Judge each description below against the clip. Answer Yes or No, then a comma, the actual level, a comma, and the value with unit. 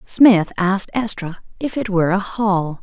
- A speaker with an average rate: Yes, average, 170 wpm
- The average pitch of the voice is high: Yes, high, 195 Hz